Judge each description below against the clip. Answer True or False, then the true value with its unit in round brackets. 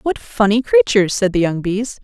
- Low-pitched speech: False (200 Hz)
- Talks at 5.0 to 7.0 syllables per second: True (5.2 syllables/s)